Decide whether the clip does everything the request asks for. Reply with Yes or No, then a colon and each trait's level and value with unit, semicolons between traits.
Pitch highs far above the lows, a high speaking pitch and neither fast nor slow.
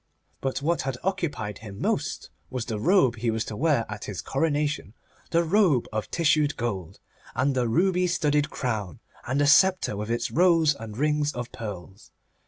No: wide, 6.0 semitones; low, 135 Hz; average, 175 wpm